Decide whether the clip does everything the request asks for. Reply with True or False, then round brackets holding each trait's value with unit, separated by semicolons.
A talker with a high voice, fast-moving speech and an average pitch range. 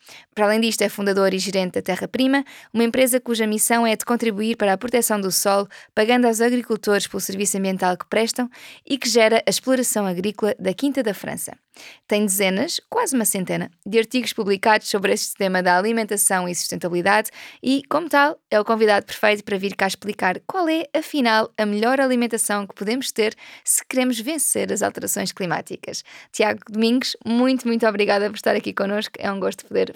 True (220 Hz; 190 wpm; 3.5 semitones)